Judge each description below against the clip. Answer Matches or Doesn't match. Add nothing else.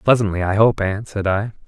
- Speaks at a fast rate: Matches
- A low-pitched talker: Matches